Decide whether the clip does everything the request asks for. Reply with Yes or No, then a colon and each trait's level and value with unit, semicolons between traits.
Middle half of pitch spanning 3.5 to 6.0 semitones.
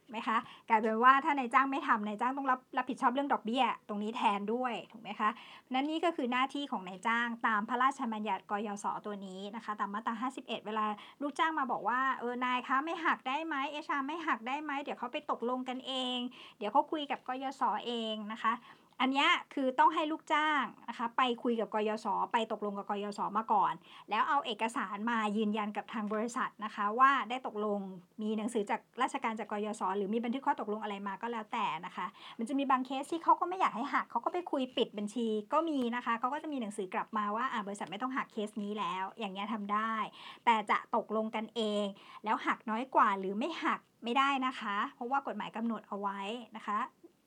Yes: average, 4.0 semitones